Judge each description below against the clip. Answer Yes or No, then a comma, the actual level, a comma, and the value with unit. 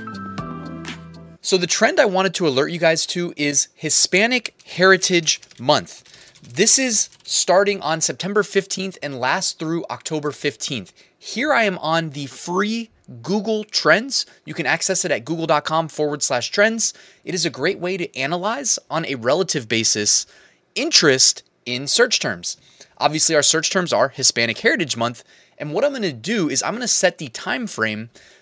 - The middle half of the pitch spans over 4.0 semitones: Yes, average, 5.1 semitones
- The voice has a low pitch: No, medium, 165 Hz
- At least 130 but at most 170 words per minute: Yes, average, 160 wpm